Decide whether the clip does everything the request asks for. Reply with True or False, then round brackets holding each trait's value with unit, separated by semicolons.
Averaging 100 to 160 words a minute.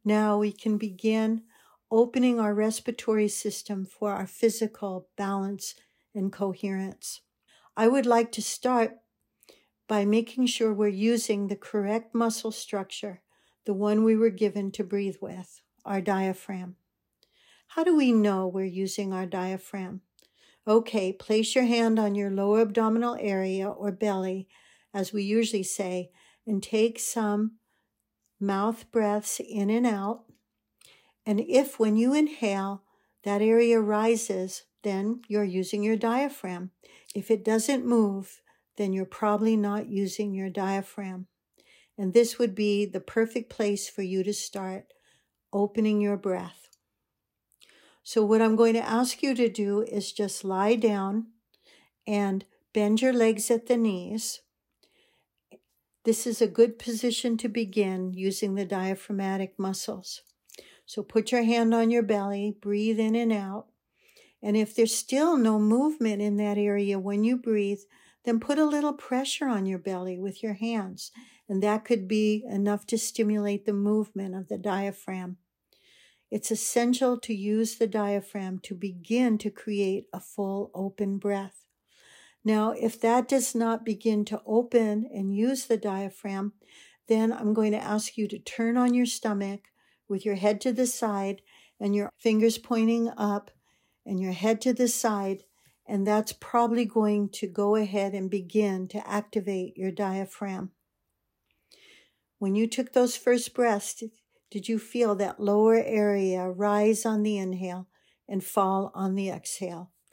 True (150 wpm)